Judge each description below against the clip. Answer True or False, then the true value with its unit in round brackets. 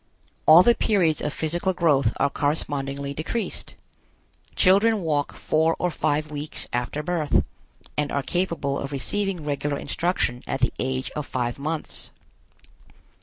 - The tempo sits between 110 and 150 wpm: True (135 wpm)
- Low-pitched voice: False (150 Hz)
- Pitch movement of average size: True (3.6 semitones)